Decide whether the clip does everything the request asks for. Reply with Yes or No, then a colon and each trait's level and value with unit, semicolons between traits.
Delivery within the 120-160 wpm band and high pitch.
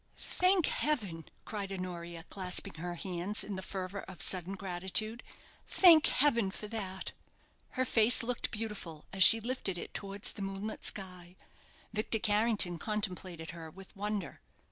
Yes: average, 145 wpm; high, 195 Hz